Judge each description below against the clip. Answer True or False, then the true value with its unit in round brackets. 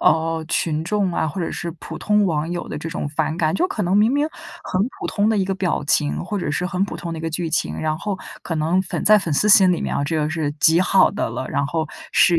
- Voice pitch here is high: False (170 Hz)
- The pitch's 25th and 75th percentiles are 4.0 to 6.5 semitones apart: False (3.6 semitones)